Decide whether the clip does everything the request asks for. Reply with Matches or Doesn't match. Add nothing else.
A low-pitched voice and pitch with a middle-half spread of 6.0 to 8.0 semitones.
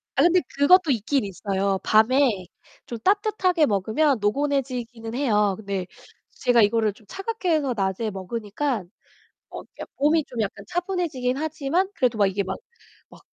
Doesn't match